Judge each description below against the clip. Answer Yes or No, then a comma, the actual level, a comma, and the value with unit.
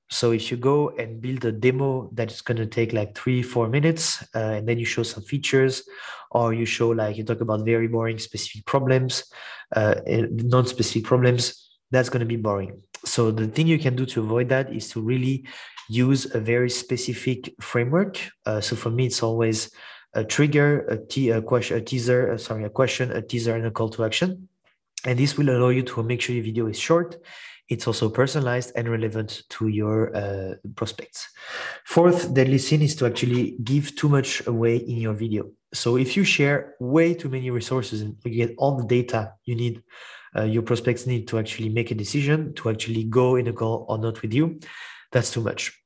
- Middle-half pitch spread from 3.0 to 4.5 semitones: No, narrow, 2.4 semitones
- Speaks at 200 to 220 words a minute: Yes, fast, 205 wpm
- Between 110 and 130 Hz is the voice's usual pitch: Yes, low, 120 Hz